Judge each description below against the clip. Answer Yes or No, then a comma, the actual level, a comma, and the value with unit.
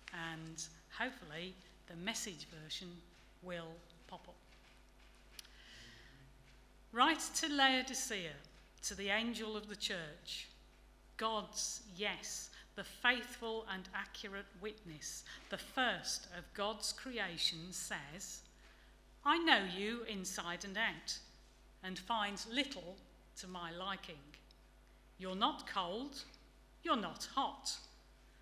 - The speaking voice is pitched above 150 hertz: Yes, high, 190 Hz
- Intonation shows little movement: No, wide, 5.4 semitones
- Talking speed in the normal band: No, slow, 100 wpm